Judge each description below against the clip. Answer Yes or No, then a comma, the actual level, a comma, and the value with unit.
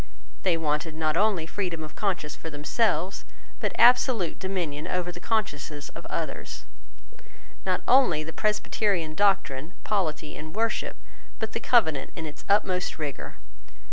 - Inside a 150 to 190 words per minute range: No, average, 140 wpm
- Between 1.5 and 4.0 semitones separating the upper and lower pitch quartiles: No, average, 4.9 semitones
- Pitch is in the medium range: Yes, medium, 175 Hz